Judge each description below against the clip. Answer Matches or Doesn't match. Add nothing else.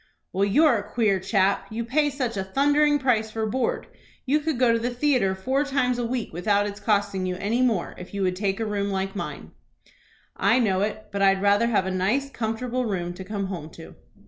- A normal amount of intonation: Matches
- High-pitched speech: Matches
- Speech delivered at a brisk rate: Matches